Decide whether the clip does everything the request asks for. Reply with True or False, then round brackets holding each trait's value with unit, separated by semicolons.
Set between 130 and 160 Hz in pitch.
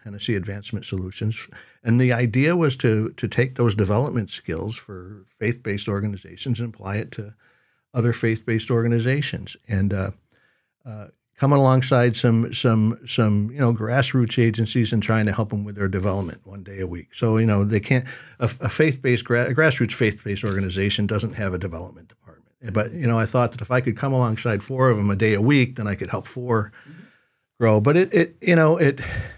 False (115 Hz)